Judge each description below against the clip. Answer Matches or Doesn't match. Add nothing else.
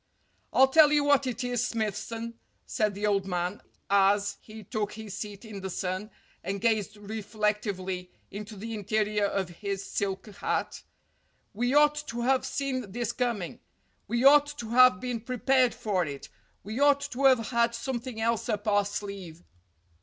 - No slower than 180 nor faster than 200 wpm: Doesn't match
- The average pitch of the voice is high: Matches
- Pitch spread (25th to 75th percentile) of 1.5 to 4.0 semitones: Matches